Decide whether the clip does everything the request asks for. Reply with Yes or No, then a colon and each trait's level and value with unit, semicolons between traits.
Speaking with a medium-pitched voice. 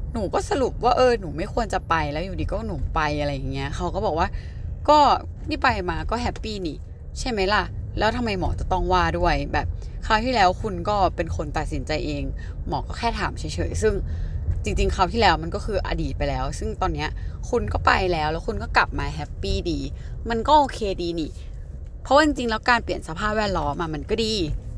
Yes: medium, 150 Hz